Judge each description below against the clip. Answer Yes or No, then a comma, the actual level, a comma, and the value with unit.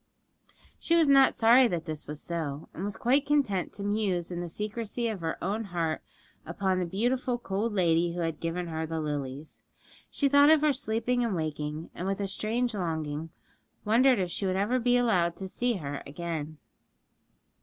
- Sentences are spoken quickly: No, average, 185 wpm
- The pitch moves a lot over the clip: Yes, wide, 6.4 semitones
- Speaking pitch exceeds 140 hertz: Yes, high, 190 Hz